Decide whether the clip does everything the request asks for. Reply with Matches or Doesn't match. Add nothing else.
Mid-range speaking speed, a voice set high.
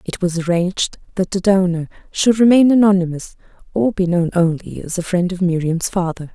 Doesn't match